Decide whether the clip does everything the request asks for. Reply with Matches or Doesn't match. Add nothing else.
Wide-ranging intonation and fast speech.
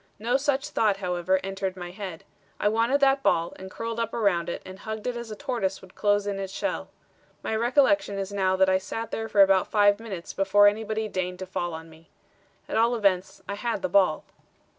Doesn't match